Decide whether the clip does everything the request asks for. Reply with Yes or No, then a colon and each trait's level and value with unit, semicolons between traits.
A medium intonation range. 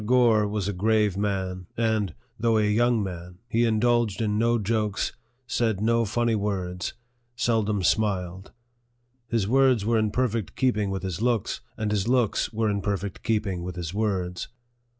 Yes: average, 3.0 semitones